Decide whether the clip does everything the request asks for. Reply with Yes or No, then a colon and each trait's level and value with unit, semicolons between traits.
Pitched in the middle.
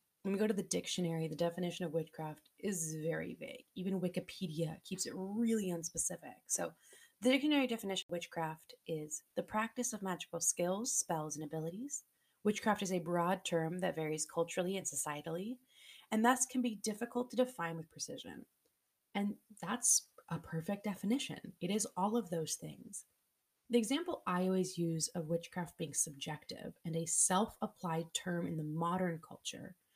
Yes: medium, 180 Hz